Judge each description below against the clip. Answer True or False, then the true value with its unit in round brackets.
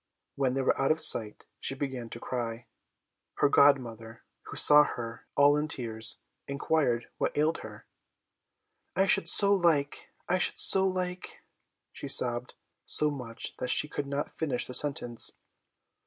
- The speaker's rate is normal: True (155 wpm)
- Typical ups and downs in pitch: True (4.1 semitones)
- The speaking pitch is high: False (140 Hz)